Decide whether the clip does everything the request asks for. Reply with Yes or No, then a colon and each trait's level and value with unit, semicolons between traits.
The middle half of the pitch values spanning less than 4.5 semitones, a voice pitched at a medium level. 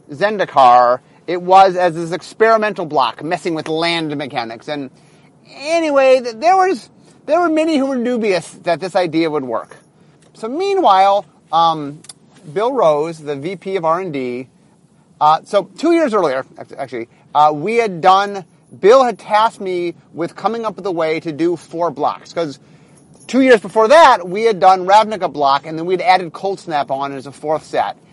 No: wide, 5.4 semitones; medium, 180 Hz